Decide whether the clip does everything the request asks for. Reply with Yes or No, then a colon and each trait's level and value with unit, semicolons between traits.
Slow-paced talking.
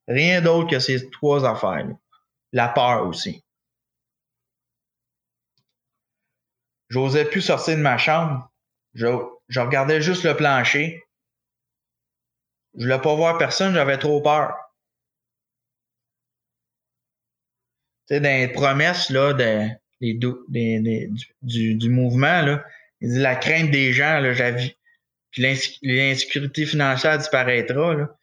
Yes: slow, 115 wpm